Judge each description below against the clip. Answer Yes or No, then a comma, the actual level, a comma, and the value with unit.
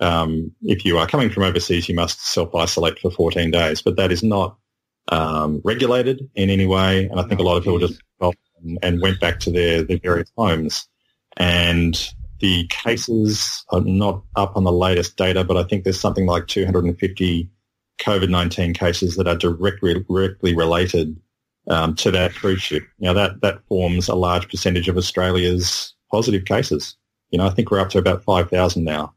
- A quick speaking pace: No, average, 180 wpm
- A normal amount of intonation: No, narrow, 2.0 semitones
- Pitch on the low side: Yes, very low, 90 Hz